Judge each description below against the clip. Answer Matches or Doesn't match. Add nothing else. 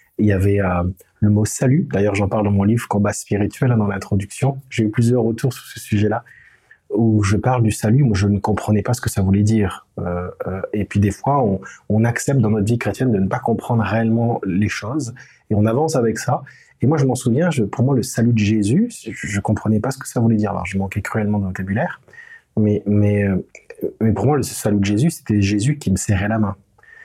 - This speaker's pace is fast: Matches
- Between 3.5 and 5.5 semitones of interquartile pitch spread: Doesn't match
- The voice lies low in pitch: Matches